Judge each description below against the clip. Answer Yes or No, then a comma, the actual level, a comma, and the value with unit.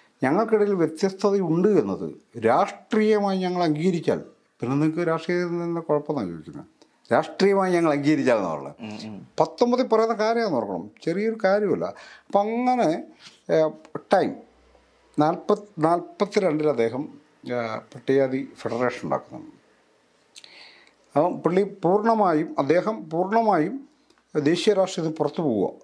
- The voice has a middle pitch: Yes, medium, 175 Hz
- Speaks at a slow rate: Yes, slow, 100 wpm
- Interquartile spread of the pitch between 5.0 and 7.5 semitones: Yes, wide, 5.4 semitones